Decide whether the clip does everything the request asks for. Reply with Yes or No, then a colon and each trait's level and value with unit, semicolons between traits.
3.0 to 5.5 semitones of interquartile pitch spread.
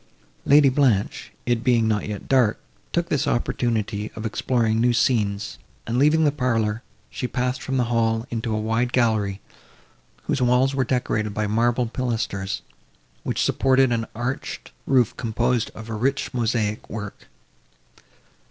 No: narrow, 2.6 semitones